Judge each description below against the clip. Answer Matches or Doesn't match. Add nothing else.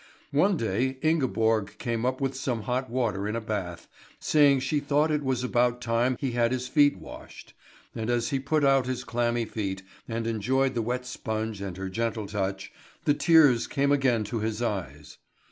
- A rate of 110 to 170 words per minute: Doesn't match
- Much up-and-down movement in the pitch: Doesn't match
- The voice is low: Matches